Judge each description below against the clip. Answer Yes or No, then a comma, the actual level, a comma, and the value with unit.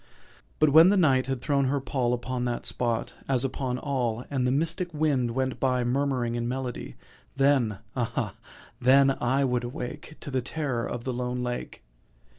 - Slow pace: No, average, 170 wpm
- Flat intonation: Yes, narrow, 2.1 semitones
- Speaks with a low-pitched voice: Yes, low, 130 Hz